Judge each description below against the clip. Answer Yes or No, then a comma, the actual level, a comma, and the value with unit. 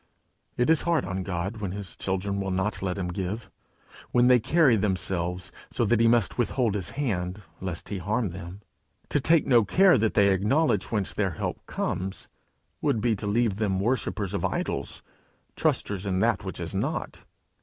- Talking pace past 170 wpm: Yes, average, 180 wpm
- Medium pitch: No, low, 100 Hz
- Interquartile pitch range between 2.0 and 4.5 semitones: Yes, average, 4.0 semitones